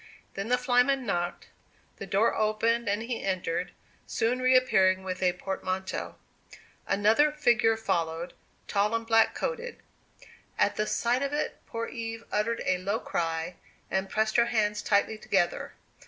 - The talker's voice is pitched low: No, high, 215 Hz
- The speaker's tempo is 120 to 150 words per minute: Yes, average, 145 wpm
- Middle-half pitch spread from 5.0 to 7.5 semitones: No, average, 3.7 semitones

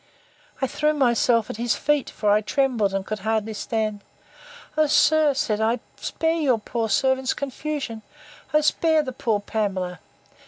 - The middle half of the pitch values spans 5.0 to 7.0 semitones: Yes, average, 5.3 semitones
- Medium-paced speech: Yes, average, 155 wpm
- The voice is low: No, high, 235 Hz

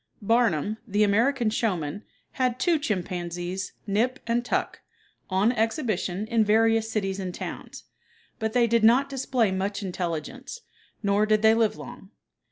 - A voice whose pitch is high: Yes, high, 220 Hz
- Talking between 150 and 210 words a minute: No, average, 140 wpm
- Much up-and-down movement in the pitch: No, average, 3.5 semitones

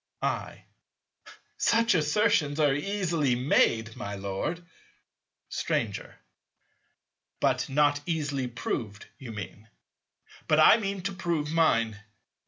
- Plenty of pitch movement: Yes, wide, 6.6 semitones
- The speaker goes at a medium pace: No, slow, 100 wpm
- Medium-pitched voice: Yes, medium, 145 Hz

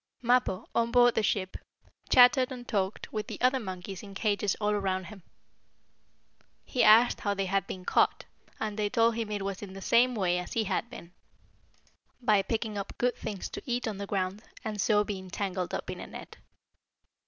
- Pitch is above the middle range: Yes, high, 210 Hz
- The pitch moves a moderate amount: Yes, average, 3.3 semitones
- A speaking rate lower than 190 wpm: No, average, 195 wpm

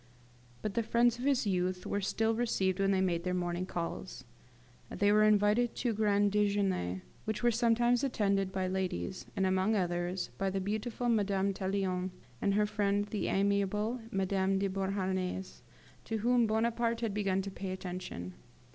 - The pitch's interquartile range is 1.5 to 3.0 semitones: Yes, narrow, 2.6 semitones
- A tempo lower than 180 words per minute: Yes, average, 165 wpm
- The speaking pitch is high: Yes, high, 200 Hz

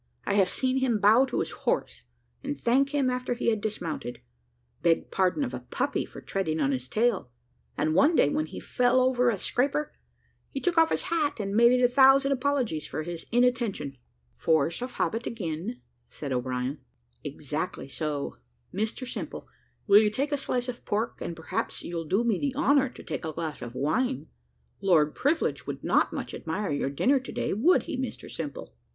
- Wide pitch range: Yes, wide, 8.2 semitones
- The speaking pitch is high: Yes, high, 220 Hz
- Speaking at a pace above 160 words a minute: Yes, average, 195 wpm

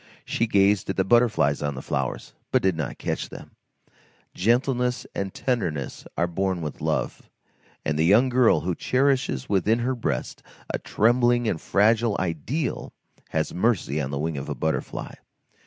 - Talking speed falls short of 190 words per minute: Yes, average, 160 wpm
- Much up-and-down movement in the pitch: Yes, wide, 7.2 semitones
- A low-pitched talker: Yes, low, 100 Hz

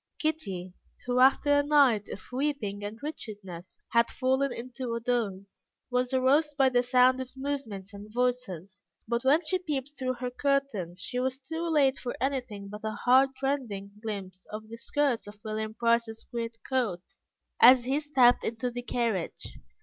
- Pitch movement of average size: Yes, average, 3.9 semitones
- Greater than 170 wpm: No, average, 165 wpm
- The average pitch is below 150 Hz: No, high, 245 Hz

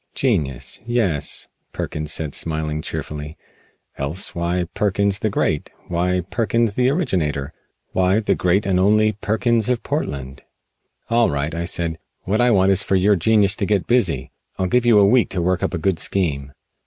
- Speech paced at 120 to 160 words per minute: No, average, 170 wpm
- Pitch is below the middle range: Yes, very low, 95 Hz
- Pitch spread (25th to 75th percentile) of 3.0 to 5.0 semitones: No, wide, 5.4 semitones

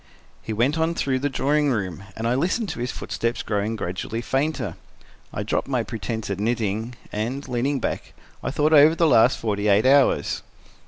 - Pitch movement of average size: Yes, average, 4.4 semitones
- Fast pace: No, average, 180 wpm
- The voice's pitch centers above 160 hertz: No, low, 120 Hz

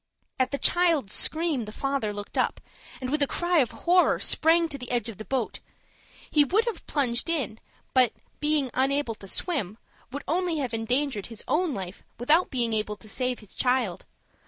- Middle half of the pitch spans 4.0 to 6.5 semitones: Yes, average, 5.3 semitones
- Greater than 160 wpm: Yes, average, 185 wpm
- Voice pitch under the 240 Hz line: No, very high, 260 Hz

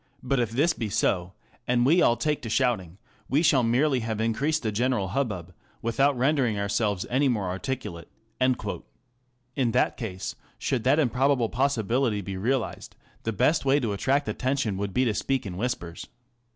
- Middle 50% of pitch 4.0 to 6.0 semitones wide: Yes, average, 4.3 semitones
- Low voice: Yes, low, 120 Hz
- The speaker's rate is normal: Yes, average, 165 wpm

